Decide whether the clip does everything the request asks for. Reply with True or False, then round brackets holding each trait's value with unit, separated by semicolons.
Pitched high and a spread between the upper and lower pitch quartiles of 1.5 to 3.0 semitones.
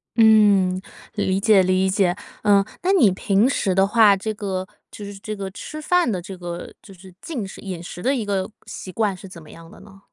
True (195 Hz; 2.4 semitones)